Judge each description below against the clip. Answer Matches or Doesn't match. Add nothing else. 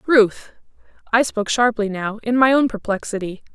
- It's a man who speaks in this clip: Doesn't match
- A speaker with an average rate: Matches